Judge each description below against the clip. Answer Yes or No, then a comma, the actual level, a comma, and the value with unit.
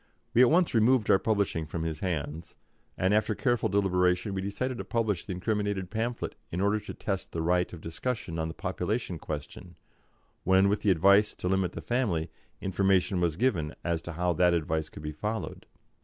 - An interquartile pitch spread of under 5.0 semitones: Yes, average, 3.8 semitones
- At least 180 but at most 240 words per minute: Yes, average, 190 wpm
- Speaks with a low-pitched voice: Yes, very low, 95 Hz